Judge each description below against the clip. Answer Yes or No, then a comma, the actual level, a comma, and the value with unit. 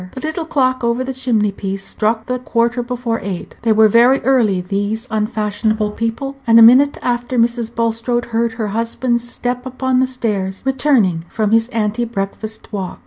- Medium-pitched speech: No, high, 230 Hz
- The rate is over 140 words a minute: Yes, average, 175 wpm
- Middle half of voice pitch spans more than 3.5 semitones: No, average, 2.7 semitones